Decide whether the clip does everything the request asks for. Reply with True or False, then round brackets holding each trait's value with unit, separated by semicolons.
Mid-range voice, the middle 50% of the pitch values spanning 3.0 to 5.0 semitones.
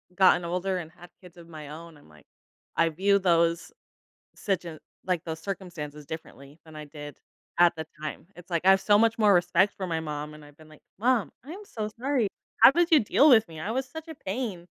True (175 Hz; 4.6 semitones)